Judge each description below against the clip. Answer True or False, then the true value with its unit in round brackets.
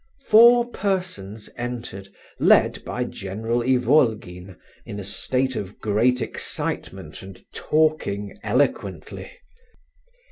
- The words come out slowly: True (95 wpm)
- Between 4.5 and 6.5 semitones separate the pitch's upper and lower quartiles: True (5.3 semitones)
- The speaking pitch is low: True (115 Hz)